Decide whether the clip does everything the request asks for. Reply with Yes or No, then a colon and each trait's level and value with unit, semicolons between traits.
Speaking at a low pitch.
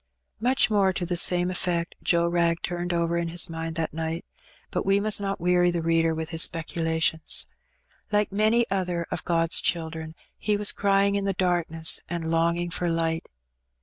No: medium, 170 Hz